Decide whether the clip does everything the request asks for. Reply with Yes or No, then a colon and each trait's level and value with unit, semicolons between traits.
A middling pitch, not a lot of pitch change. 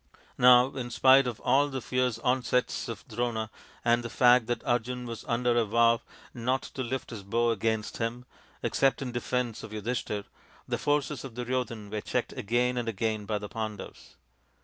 No: low, 120 Hz; narrow, 1.9 semitones